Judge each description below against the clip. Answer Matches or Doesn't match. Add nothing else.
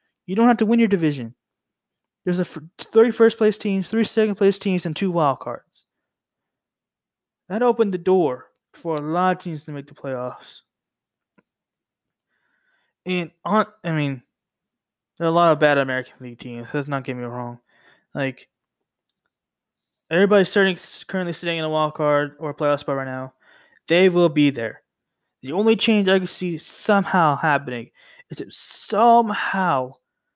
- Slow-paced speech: Doesn't match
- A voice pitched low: Doesn't match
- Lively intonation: Matches